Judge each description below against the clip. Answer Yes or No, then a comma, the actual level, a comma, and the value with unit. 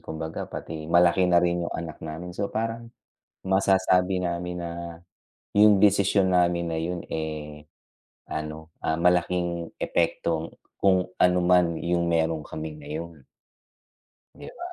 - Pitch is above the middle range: No, very low, 85 Hz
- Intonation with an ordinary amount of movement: No, narrow, 2.2 semitones